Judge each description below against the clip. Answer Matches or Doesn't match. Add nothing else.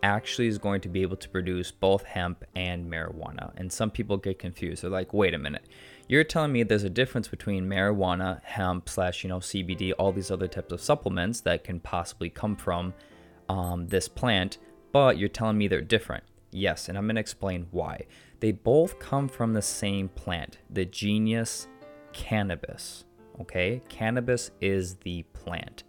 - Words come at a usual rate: Matches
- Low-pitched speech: Matches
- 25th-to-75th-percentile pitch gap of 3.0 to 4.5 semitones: Matches